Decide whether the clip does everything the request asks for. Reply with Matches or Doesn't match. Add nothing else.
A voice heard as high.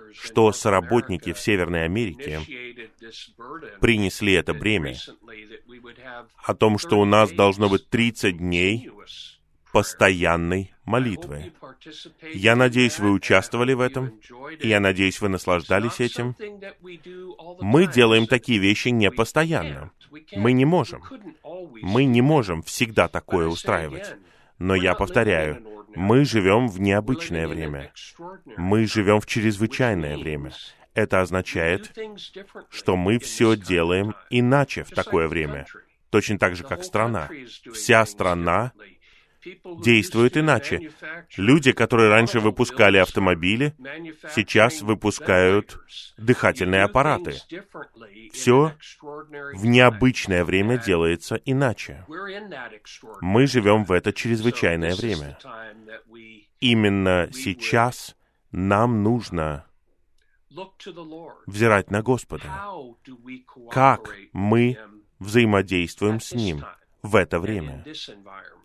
Doesn't match